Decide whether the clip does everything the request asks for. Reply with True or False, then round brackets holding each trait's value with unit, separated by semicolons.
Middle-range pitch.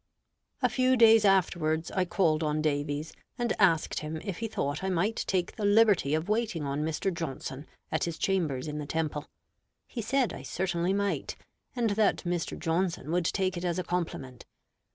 True (175 Hz)